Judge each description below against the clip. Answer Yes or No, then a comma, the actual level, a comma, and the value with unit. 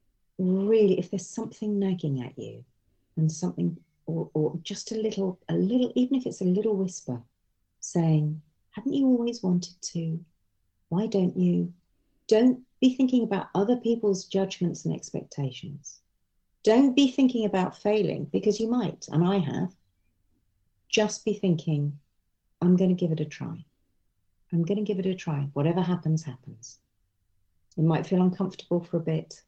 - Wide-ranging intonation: Yes, wide, 7.2 semitones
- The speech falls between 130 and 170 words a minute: Yes, average, 160 wpm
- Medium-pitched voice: Yes, medium, 175 Hz